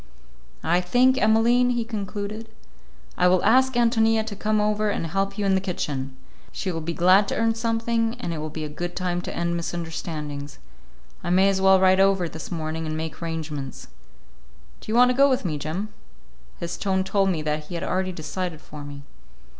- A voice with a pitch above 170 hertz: Yes, medium, 185 Hz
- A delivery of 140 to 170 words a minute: No, average, 200 wpm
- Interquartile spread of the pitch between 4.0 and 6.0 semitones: Yes, average, 4.9 semitones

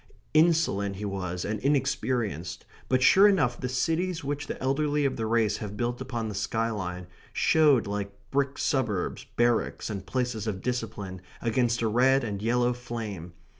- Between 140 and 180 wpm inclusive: Yes, average, 160 wpm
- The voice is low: Yes, low, 120 Hz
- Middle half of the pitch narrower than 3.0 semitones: No, average, 4.6 semitones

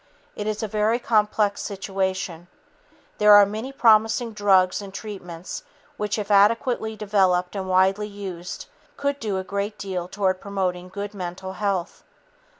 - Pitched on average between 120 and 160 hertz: No, high, 200 Hz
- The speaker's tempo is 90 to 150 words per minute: Yes, average, 145 wpm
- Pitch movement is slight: Yes, narrow, 2.2 semitones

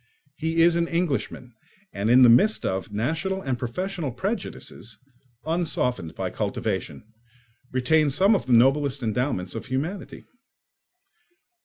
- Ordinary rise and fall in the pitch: No, wide, 5.9 semitones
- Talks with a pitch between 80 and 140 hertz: Yes, low, 135 Hz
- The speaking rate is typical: No, slow, 125 wpm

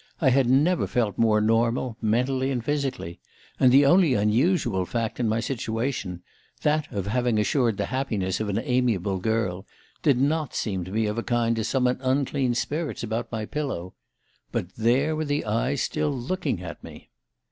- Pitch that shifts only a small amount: No, average, 4.2 semitones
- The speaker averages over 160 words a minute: Yes, average, 170 wpm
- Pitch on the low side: Yes, low, 120 Hz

